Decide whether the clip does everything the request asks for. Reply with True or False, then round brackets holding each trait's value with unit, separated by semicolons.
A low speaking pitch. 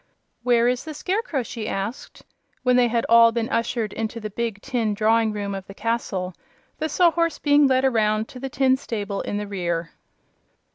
False (230 Hz)